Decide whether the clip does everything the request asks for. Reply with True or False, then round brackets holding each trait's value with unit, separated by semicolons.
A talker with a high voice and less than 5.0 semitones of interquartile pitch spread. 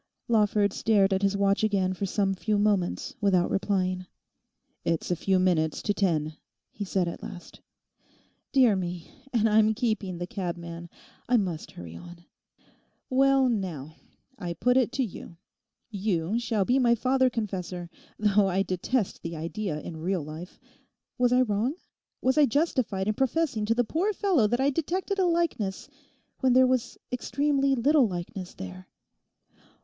False (205 Hz; 5.6 semitones)